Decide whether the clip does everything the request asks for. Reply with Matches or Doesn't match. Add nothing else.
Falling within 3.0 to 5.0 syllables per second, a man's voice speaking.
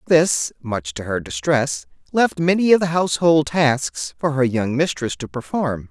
Matches